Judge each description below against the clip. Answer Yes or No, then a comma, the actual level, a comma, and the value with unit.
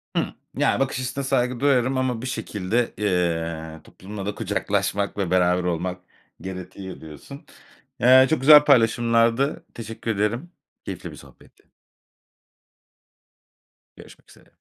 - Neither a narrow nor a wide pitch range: No, wide, 5.7 semitones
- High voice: No, low, 110 Hz